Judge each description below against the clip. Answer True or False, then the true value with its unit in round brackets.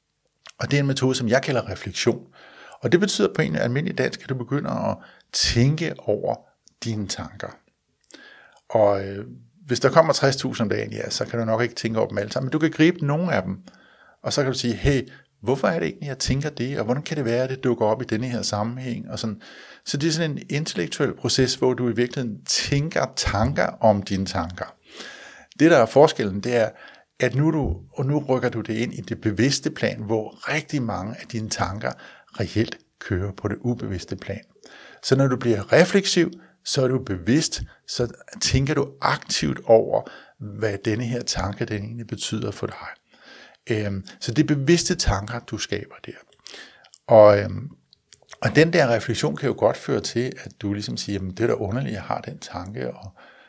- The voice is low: True (120 Hz)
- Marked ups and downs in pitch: False (4.3 semitones)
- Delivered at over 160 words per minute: True (205 wpm)